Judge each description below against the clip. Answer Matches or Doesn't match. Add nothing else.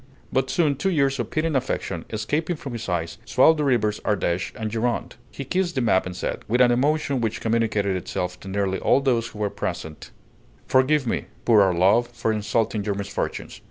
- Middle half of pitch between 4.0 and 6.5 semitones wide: Matches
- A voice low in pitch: Matches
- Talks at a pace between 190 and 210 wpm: Matches